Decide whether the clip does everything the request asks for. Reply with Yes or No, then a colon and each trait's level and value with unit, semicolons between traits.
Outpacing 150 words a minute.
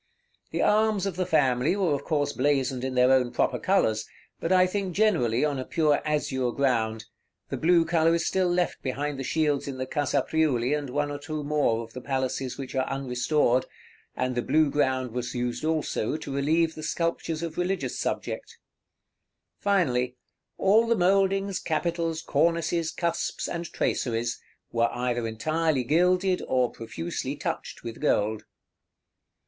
Yes: average, 160 wpm